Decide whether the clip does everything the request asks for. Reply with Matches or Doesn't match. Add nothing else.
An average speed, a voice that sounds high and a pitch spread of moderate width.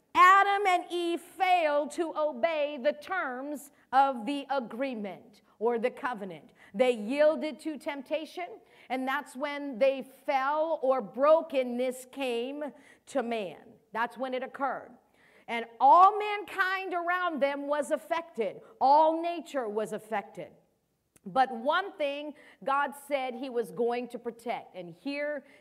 Doesn't match